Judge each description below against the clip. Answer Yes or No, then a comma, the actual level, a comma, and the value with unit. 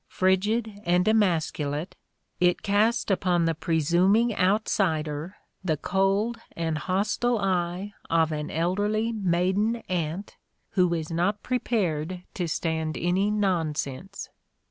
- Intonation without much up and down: No, average, 3.8 semitones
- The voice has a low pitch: No, medium, 185 Hz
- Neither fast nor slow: No, slow, 115 wpm